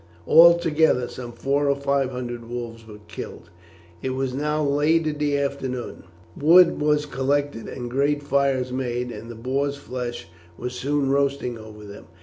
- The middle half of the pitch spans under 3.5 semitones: Yes, average, 2.8 semitones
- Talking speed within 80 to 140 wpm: No, average, 155 wpm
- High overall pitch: No, low, 135 Hz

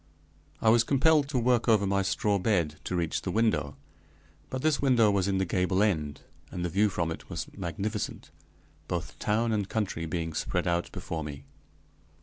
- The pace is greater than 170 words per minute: Yes, average, 180 wpm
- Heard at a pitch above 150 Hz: No, low, 100 Hz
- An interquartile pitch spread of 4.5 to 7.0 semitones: Yes, average, 4.8 semitones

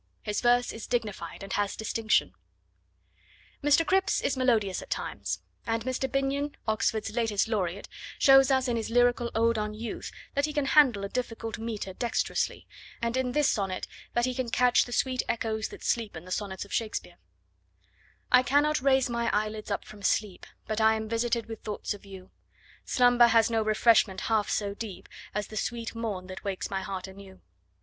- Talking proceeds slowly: No, average, 185 wpm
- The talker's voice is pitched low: No, high, 225 Hz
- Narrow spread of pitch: No, average, 3.0 semitones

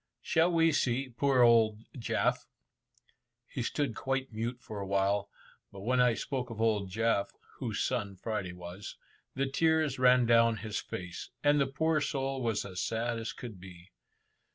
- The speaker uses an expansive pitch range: No, average, 4.6 semitones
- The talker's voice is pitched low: Yes, low, 115 Hz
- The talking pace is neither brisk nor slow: Yes, average, 165 wpm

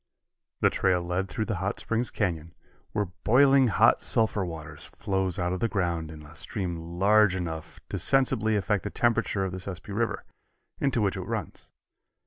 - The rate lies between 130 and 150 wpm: No, average, 175 wpm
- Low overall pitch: Yes, very low, 95 Hz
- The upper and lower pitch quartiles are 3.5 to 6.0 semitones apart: Yes, average, 4.0 semitones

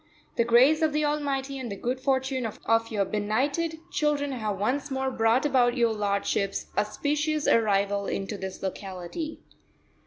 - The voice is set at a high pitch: Yes, high, 245 Hz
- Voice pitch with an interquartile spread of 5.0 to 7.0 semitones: Yes, wide, 5.5 semitones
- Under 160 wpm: Yes, average, 150 wpm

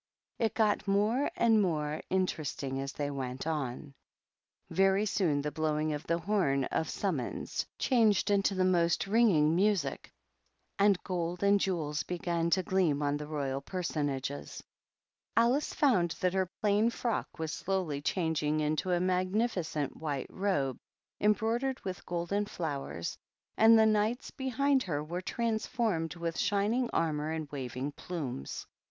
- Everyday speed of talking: Yes, average, 145 wpm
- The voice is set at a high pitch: No, medium, 175 Hz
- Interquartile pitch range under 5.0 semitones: No, wide, 5.5 semitones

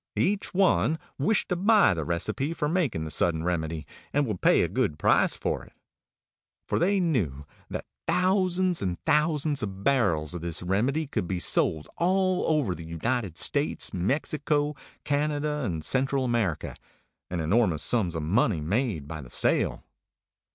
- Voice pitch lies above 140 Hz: No, low, 120 Hz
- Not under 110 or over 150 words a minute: No, average, 160 wpm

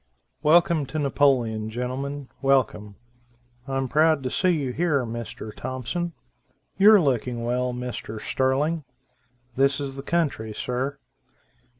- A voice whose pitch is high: No, low, 135 Hz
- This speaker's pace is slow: Yes, slow, 125 wpm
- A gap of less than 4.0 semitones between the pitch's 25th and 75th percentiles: Yes, average, 3.4 semitones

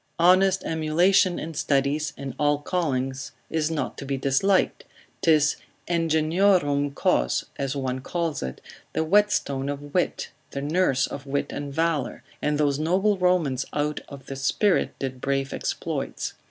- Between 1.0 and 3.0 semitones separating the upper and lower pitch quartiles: No, average, 3.7 semitones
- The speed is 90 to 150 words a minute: Yes, average, 145 wpm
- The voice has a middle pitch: Yes, medium, 150 Hz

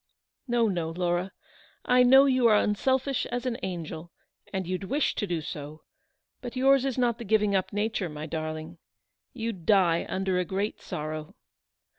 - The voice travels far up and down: Yes, wide, 6.2 semitones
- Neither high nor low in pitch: No, high, 195 Hz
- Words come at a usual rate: Yes, average, 165 wpm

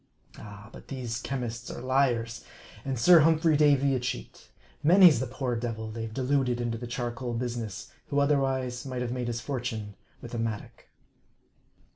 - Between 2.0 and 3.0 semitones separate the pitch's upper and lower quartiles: Yes, average, 2.7 semitones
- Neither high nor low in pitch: No, low, 125 Hz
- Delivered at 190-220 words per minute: No, average, 165 wpm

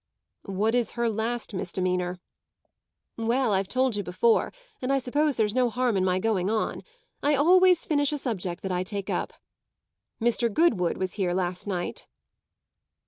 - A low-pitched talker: No, high, 220 Hz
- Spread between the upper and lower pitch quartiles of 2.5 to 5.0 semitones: No, wide, 5.4 semitones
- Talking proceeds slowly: No, average, 160 wpm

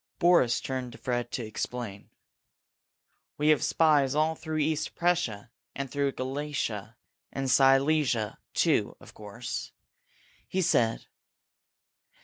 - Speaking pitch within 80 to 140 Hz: Yes, low, 135 Hz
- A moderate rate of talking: No, slow, 115 wpm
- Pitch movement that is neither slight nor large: Yes, average, 4.4 semitones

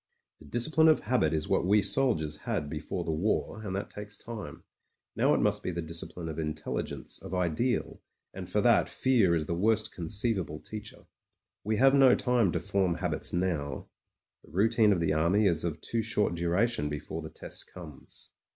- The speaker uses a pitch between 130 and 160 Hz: No, very low, 90 Hz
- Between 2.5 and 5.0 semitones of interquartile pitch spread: No, wide, 5.4 semitones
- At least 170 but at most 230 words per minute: Yes, average, 190 wpm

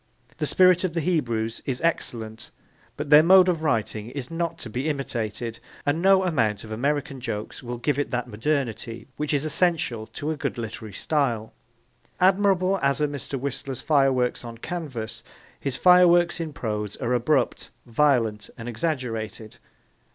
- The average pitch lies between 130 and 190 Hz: Yes, low, 135 Hz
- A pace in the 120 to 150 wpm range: No, average, 160 wpm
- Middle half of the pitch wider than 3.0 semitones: Yes, wide, 5.4 semitones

